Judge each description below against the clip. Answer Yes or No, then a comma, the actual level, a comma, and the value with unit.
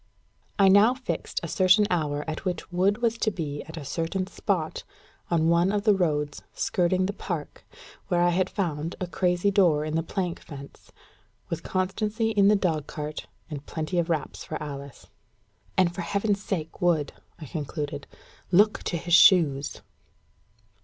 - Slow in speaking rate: No, average, 165 wpm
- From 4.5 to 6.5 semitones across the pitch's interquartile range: No, average, 4.0 semitones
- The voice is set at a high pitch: No, medium, 175 Hz